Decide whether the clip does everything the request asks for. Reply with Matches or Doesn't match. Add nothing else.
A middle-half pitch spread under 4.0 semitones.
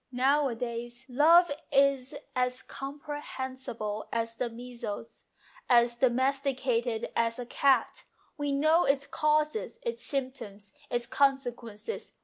Matches